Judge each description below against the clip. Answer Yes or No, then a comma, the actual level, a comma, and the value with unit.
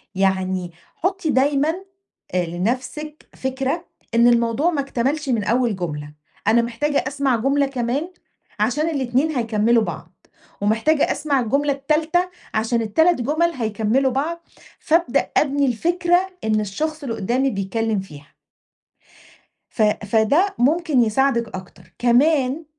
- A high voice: Yes, very high, 260 Hz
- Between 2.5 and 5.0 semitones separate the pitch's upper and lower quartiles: No, wide, 5.4 semitones